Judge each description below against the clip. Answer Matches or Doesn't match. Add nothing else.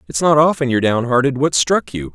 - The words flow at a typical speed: Doesn't match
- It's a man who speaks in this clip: Matches